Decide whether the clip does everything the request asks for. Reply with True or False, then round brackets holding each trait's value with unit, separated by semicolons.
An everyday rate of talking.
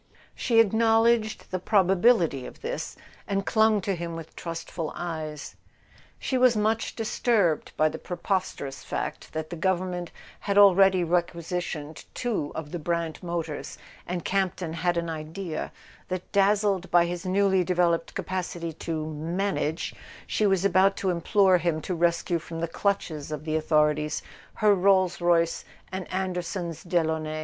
True (150 wpm)